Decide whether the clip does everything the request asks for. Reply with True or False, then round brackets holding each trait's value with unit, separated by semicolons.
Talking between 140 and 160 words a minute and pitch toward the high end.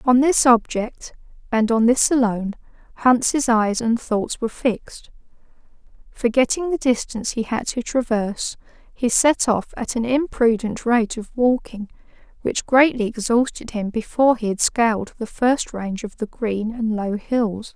True (155 wpm; 235 Hz)